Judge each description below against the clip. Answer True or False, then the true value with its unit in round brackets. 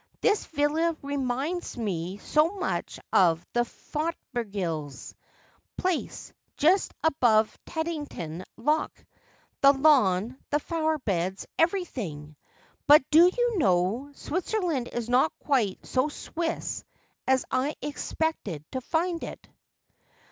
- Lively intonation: True (7.3 semitones)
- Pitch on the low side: False (275 Hz)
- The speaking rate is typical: False (110 wpm)